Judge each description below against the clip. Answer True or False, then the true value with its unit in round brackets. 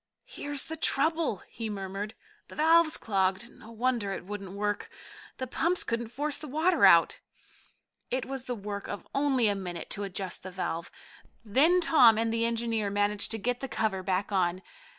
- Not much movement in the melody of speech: False (5.3 semitones)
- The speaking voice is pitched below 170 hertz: False (225 Hz)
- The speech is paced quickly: False (175 wpm)